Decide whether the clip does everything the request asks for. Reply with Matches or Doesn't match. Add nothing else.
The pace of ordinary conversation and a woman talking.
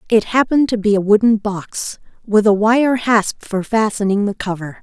Matches